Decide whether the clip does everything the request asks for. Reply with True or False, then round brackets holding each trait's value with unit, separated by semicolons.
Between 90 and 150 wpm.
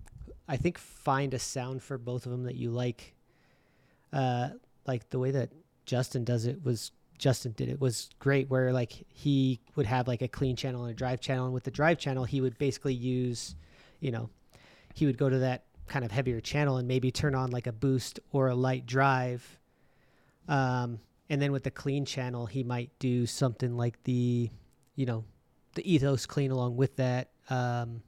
False (195 wpm)